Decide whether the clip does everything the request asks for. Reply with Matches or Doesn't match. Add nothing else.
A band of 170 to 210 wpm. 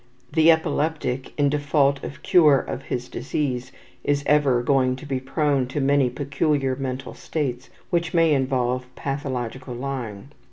Doesn't match